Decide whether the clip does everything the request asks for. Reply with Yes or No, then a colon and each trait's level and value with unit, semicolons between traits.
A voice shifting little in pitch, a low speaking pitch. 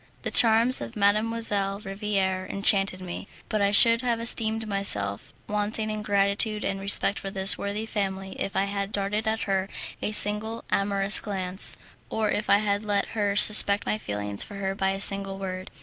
No: narrow, 1.7 semitones; high, 200 Hz